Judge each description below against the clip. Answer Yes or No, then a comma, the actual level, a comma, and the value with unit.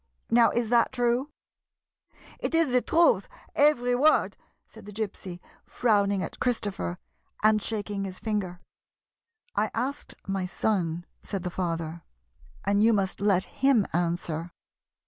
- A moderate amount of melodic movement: Yes, average, 5.0 semitones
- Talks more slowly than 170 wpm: Yes, average, 145 wpm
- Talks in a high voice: Yes, high, 205 Hz